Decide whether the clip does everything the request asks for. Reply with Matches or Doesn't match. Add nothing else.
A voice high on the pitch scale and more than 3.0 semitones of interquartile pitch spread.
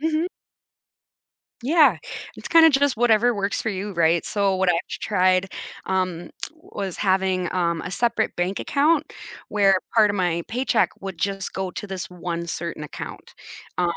Matches